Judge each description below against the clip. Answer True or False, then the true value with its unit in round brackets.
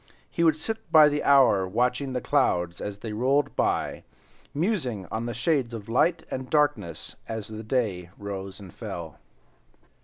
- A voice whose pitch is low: True (120 Hz)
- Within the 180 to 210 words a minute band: False (160 wpm)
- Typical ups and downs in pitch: False (6.1 semitones)